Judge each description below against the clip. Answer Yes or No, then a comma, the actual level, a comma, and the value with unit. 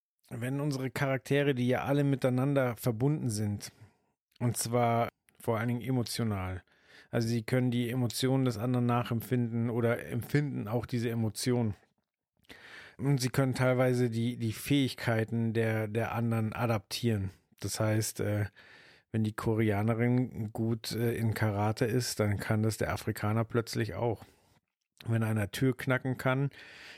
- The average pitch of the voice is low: Yes, low, 120 Hz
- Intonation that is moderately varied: No, narrow, 2.3 semitones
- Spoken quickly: No, average, 135 wpm